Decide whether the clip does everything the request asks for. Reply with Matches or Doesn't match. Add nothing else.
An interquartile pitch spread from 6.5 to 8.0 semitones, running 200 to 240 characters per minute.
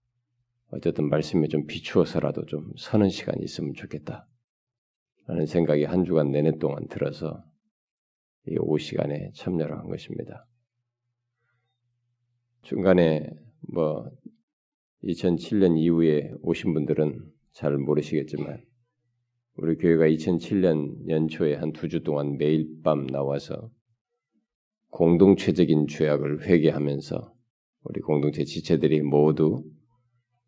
Matches